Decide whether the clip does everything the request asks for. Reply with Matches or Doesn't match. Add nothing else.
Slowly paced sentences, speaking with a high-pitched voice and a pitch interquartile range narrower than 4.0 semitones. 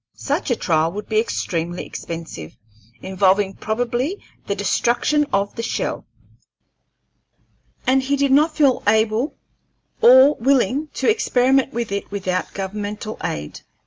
Doesn't match